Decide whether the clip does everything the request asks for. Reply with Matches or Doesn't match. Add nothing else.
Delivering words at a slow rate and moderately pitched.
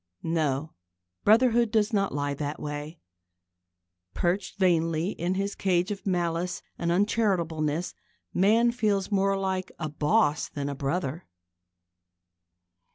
Matches